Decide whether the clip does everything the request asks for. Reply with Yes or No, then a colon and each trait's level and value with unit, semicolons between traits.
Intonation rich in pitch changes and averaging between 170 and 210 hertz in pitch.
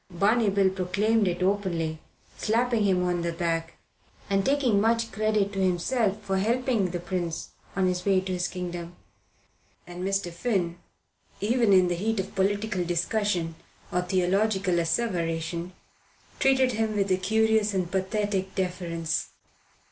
No: average, 3.3 semitones; high, 190 Hz